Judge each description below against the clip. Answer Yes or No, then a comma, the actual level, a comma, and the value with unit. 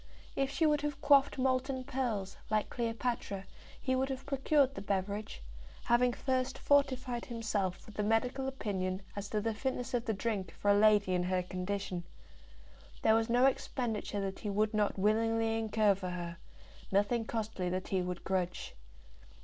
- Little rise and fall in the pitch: No, average, 4.5 semitones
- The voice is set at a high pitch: Yes, high, 220 Hz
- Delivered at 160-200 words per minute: Yes, average, 165 wpm